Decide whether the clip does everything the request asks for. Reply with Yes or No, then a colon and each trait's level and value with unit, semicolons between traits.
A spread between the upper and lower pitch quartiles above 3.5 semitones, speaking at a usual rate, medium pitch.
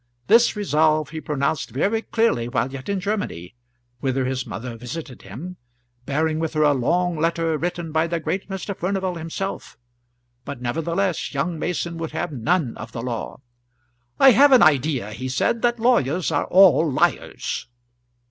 Yes: wide, 5.4 semitones; average, 160 wpm; medium, 160 Hz